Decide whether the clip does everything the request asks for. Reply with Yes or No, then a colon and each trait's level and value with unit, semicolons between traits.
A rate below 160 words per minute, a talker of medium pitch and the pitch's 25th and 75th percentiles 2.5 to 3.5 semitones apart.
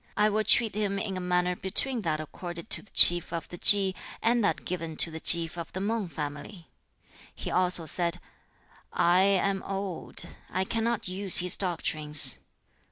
No: average, 170 wpm; medium, 180 Hz; average, 2.9 semitones